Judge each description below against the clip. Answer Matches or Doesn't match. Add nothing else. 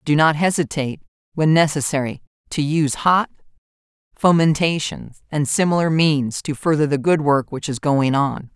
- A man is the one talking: Doesn't match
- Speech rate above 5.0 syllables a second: Doesn't match